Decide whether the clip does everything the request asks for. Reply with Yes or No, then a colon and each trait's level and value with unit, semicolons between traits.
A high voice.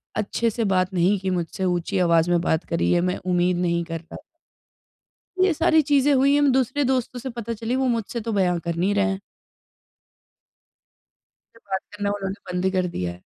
Yes: high, 195 Hz